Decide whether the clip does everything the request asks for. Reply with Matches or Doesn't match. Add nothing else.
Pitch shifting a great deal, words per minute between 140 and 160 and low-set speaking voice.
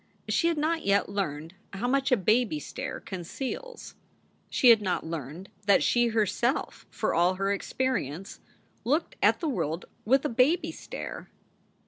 Doesn't match